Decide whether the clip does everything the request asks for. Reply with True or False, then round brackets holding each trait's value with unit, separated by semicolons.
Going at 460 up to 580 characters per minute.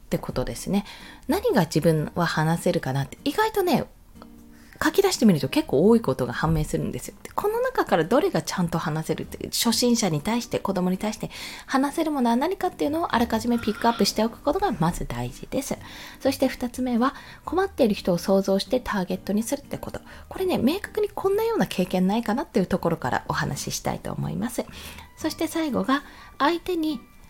False (430 characters per minute)